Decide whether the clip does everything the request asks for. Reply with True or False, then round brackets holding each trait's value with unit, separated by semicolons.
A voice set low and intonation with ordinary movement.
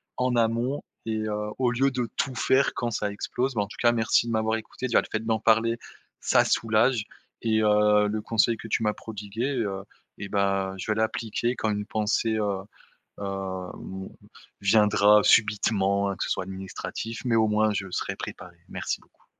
False (110 Hz; 2.1 semitones)